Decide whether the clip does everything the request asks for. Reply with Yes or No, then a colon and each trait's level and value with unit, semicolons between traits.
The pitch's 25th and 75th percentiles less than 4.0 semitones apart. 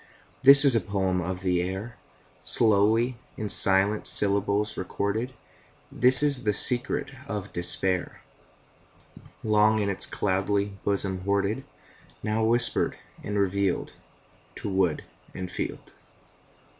Yes: narrow, 2.5 semitones